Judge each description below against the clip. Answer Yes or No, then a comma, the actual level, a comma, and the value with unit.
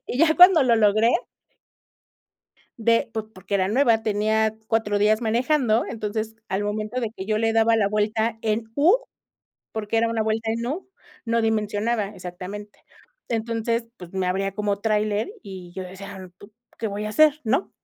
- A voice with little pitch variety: Yes, narrow, 2.0 semitones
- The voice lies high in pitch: Yes, high, 220 Hz